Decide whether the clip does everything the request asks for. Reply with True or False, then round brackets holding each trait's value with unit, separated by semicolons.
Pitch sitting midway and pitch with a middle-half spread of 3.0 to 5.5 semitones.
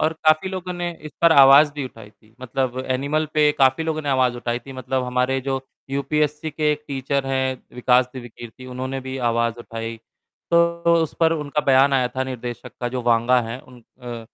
False (130 Hz; 3.3 semitones)